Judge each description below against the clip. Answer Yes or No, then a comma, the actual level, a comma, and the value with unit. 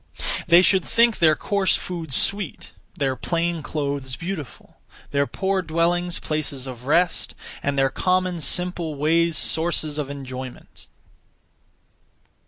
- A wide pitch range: No, average, 4.0 semitones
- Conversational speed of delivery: No, slow, 120 wpm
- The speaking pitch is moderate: Yes, medium, 160 Hz